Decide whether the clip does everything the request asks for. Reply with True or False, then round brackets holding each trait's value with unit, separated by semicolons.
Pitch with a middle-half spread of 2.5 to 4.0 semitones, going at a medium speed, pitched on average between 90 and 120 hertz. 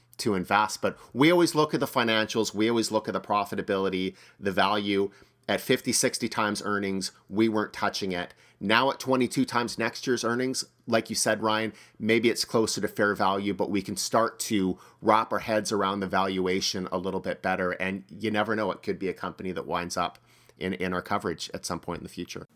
False (2.8 semitones; 215 wpm; 105 Hz)